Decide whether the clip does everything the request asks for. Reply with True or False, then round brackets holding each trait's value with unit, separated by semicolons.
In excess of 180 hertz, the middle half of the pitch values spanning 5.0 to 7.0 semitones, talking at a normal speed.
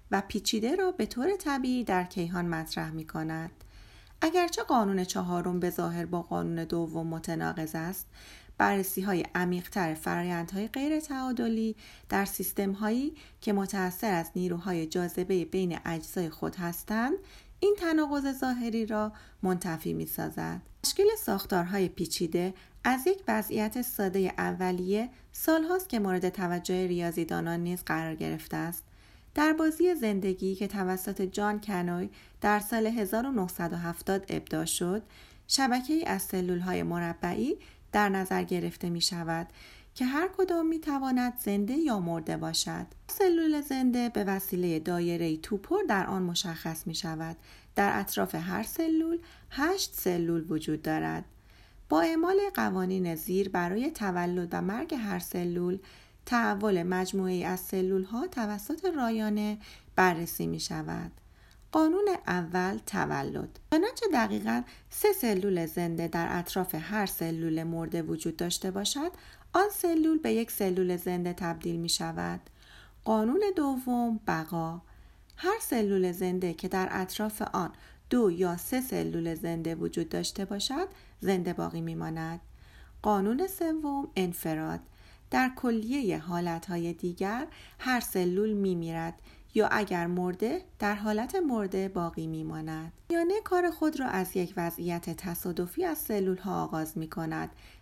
True (190 Hz; 5.6 semitones; 130 wpm)